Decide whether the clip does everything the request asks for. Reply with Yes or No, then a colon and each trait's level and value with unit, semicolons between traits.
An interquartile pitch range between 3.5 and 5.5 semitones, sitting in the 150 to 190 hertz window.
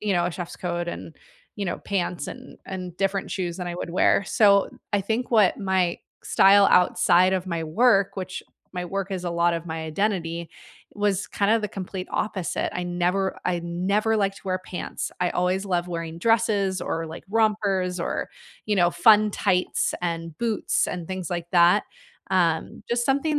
No: narrow, 2.6 semitones; medium, 185 Hz